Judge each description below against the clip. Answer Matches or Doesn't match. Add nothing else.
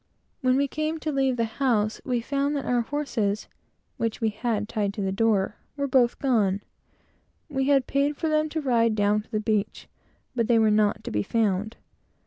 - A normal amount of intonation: Matches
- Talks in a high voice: Matches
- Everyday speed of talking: Matches